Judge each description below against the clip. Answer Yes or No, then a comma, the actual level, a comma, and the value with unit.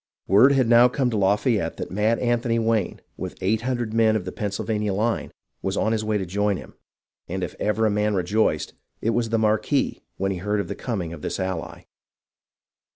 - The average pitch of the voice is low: Yes, low, 105 Hz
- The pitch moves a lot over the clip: No, average, 2.7 semitones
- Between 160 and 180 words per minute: No, fast, 205 wpm